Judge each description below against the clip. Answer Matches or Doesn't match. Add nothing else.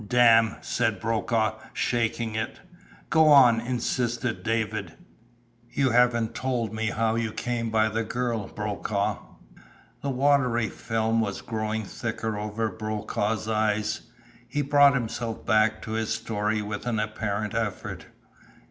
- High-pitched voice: Doesn't match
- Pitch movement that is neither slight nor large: Doesn't match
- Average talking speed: Doesn't match